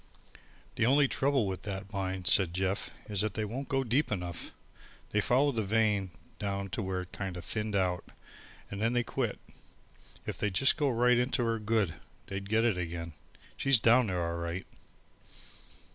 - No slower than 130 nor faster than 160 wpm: No, average, 175 wpm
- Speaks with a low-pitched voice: Yes, low, 105 Hz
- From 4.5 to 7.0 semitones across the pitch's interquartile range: No, average, 4.0 semitones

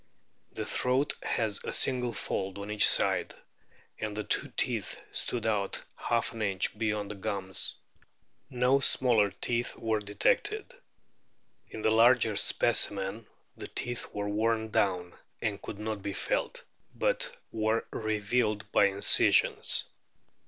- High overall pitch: No, low, 110 Hz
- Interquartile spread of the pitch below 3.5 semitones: Yes, average, 2.9 semitones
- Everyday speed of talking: No, slow, 130 wpm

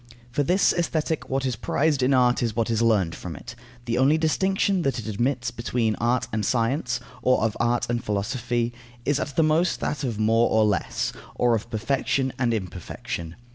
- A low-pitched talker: Yes, low, 120 Hz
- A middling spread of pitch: Yes, average, 3.6 semitones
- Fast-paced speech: No, average, 185 wpm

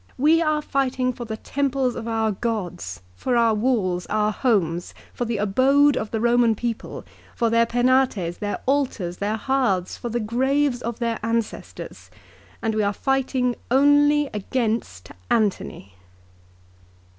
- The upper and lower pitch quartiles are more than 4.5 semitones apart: No, average, 3.7 semitones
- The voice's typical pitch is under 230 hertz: No, high, 235 Hz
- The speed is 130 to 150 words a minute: Yes, average, 145 wpm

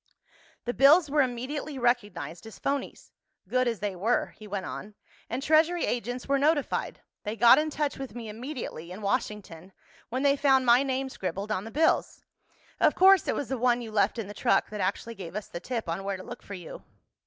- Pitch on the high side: Yes, high, 240 Hz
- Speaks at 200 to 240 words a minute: Yes, fast, 205 wpm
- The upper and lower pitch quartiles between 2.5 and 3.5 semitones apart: No, average, 4.9 semitones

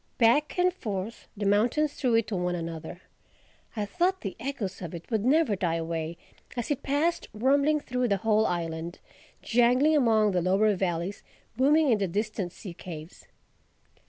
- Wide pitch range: Yes, wide, 6.6 semitones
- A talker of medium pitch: No, high, 215 Hz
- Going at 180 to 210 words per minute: No, average, 165 wpm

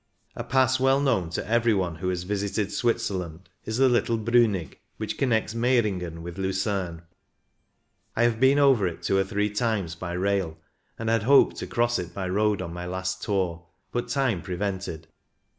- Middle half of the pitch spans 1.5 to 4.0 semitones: No, average, 4.5 semitones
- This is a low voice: Yes, low, 100 Hz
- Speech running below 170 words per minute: No, average, 175 wpm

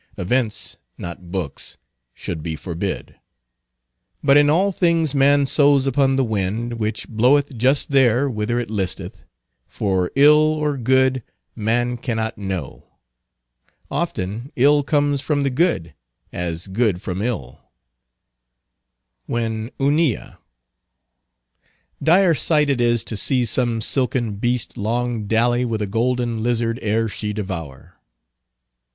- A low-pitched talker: Yes, low, 120 Hz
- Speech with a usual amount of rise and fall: Yes, average, 4.7 semitones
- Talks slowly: Yes, slow, 120 wpm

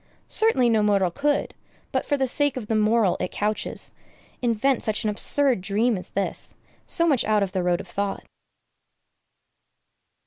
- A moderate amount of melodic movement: Yes, average, 4.7 semitones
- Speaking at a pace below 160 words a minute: No, average, 165 wpm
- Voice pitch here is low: No, high, 215 Hz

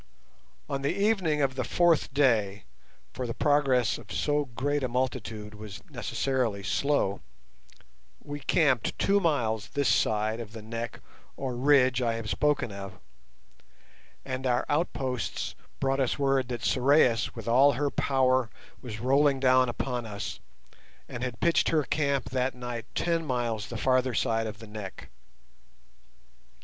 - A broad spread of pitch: No, average, 3.6 semitones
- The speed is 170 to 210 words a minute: No, average, 145 wpm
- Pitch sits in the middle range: No, low, 130 Hz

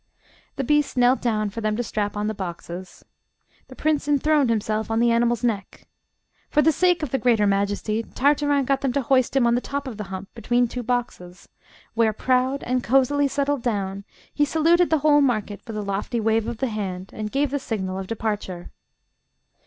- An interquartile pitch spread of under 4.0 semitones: No, average, 4.6 semitones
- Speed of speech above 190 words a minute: Yes, average, 200 wpm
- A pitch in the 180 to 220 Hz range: No, high, 235 Hz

